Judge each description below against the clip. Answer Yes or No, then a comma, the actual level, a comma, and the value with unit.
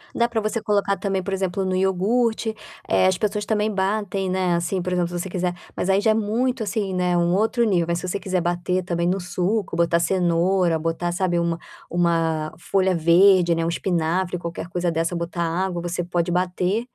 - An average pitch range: No, narrow, 2.3 semitones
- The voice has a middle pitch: Yes, medium, 180 Hz